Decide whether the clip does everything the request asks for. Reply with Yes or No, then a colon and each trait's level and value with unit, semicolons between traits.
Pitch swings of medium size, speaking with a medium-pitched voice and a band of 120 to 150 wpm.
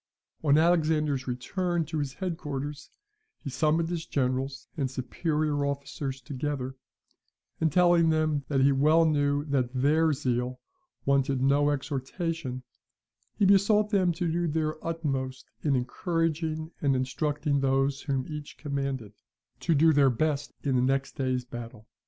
Yes: average, 3.2 semitones; medium, 145 Hz; average, 140 wpm